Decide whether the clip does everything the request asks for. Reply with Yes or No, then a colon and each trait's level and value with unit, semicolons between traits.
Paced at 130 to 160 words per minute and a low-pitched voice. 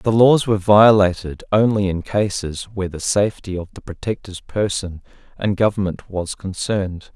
Yes: average, 150 wpm; low, 100 Hz